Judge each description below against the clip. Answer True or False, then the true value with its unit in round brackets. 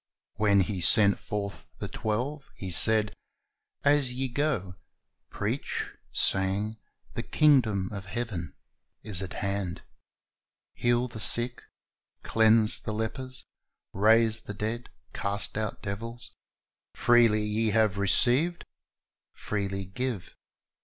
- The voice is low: True (110 Hz)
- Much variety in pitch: False (3.2 semitones)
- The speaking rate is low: True (110 wpm)